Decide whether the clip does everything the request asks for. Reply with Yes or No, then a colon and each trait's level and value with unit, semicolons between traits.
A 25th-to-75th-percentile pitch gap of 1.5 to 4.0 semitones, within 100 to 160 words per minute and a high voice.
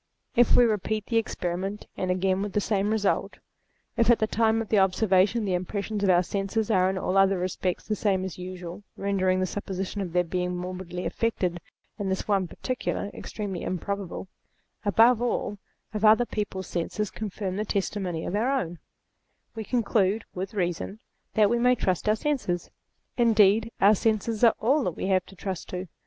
No: average, 2.9 semitones; average, 185 wpm; high, 200 Hz